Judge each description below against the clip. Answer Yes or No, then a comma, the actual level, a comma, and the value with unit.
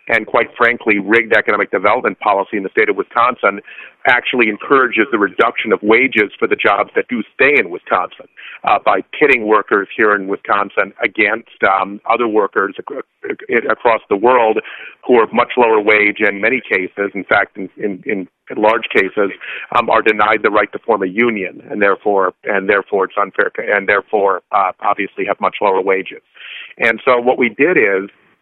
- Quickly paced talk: No, average, 175 wpm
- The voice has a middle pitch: No, low, 115 Hz